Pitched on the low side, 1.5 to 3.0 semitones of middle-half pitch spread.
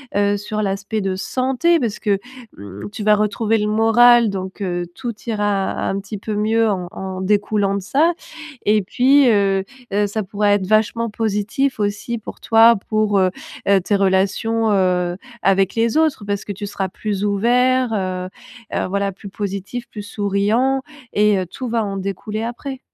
No: high, 205 Hz; narrow, 2.5 semitones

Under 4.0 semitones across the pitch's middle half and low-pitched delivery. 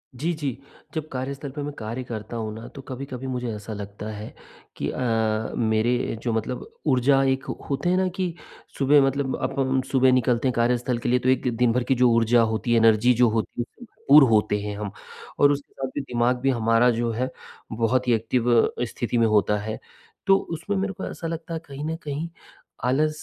Yes: average, 3.3 semitones; low, 125 Hz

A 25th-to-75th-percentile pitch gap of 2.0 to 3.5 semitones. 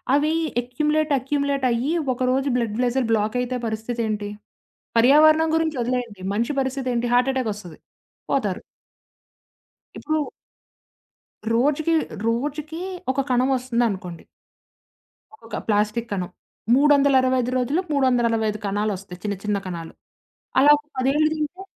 No: average, 4.5 semitones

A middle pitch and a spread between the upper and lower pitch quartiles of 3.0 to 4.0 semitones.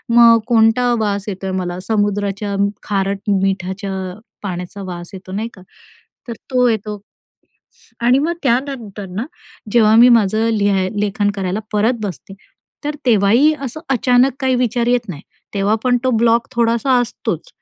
No: high, 220 Hz; average, 3.7 semitones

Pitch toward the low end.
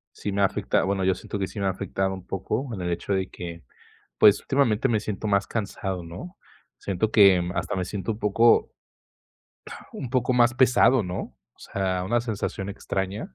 Yes: low, 100 Hz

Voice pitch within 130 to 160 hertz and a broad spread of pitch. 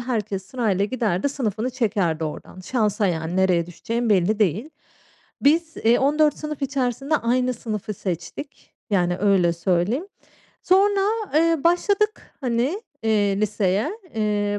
No: high, 220 Hz; wide, 6.0 semitones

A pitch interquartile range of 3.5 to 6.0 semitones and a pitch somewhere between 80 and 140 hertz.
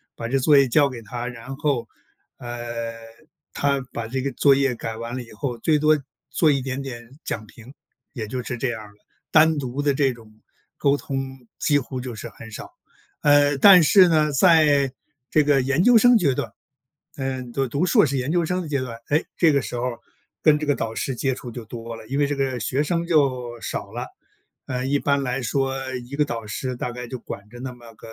No: average, 3.1 semitones; low, 135 Hz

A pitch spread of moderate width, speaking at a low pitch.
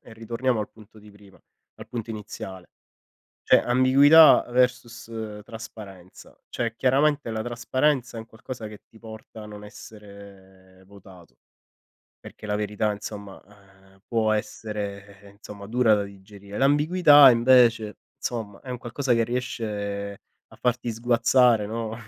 Yes: average, 3.1 semitones; low, 110 Hz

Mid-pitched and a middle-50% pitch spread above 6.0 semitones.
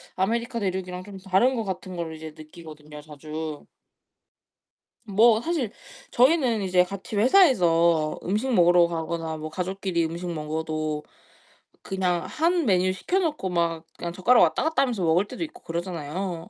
No: medium, 180 Hz; average, 5.1 semitones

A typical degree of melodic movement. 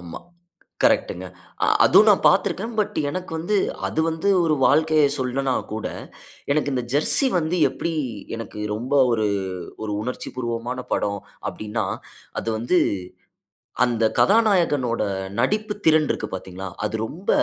No: wide, 6.2 semitones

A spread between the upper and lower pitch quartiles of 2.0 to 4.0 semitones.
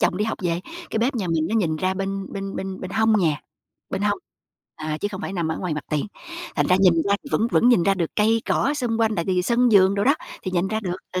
Yes: average, 3.6 semitones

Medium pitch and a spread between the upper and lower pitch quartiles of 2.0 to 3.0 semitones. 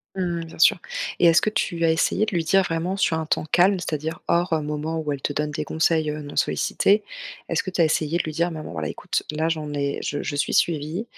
Yes: medium, 160 Hz; narrow, 2.4 semitones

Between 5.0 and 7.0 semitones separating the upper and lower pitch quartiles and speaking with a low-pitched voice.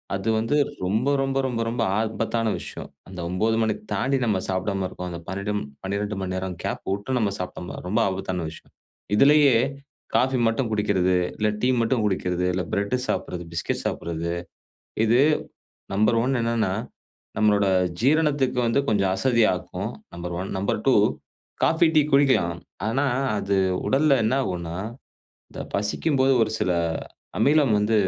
Yes: average, 5.3 semitones; low, 105 Hz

